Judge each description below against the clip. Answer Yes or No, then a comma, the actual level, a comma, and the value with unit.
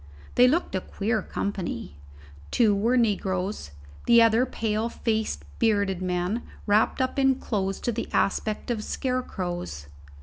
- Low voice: No, high, 215 Hz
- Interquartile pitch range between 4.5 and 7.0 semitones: No, average, 3.6 semitones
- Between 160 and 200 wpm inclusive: No, slow, 135 wpm